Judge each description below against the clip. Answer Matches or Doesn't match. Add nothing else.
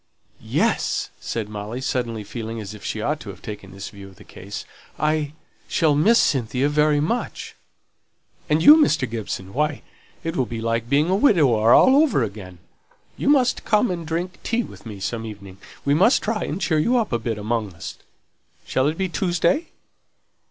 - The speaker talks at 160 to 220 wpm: Matches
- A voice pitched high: Doesn't match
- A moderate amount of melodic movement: Doesn't match